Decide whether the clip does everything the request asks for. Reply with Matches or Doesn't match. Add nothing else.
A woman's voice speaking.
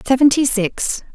Matches